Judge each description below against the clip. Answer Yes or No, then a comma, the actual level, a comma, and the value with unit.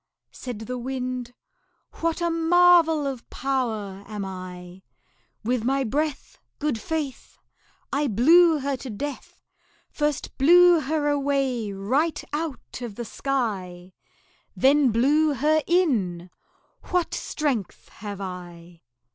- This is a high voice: Yes, very high, 265 Hz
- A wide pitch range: Yes, wide, 6.3 semitones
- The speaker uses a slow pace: Yes, slow, 115 wpm